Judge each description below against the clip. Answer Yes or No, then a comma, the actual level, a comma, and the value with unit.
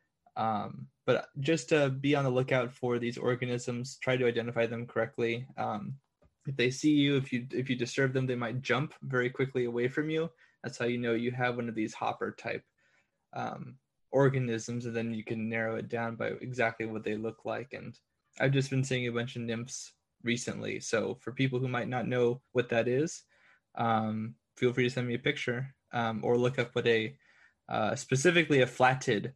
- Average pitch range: No, narrow, 2.0 semitones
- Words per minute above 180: Yes, average, 200 wpm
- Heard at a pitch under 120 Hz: No, low, 125 Hz